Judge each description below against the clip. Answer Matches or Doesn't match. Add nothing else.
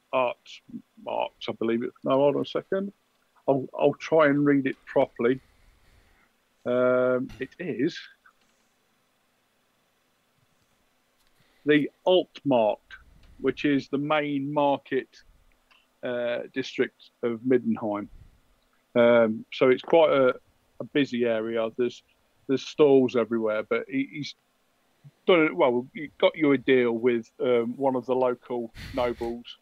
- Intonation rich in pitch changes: Doesn't match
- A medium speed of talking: Doesn't match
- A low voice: Matches